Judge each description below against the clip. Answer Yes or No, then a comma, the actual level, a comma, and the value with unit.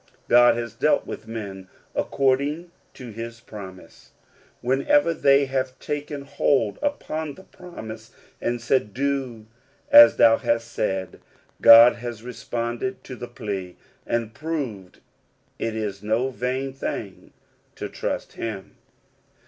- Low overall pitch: Yes, low, 120 Hz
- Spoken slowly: Yes, slow, 125 wpm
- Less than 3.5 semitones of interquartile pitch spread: No, average, 3.8 semitones